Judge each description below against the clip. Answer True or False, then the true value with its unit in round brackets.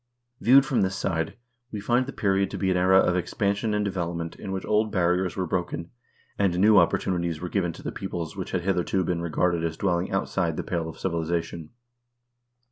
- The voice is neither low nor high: False (90 Hz)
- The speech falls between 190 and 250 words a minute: True (200 wpm)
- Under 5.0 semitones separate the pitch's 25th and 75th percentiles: True (2.6 semitones)